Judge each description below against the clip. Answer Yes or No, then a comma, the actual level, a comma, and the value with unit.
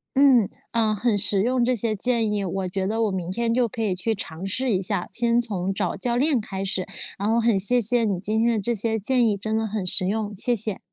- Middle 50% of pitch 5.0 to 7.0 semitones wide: No, average, 3.4 semitones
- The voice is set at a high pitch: Yes, high, 220 Hz